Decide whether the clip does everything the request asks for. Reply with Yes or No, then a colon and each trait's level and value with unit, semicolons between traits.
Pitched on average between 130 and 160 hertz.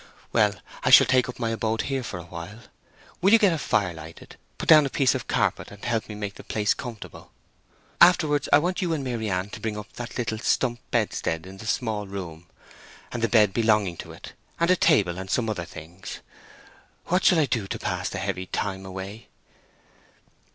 No: low, 110 Hz